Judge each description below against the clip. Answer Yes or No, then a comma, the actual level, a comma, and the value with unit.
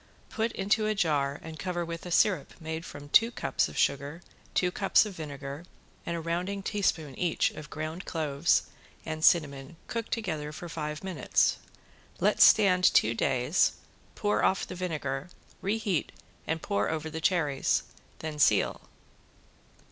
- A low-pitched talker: No, medium, 160 Hz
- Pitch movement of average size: Yes, average, 3.7 semitones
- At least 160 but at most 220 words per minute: No, average, 150 wpm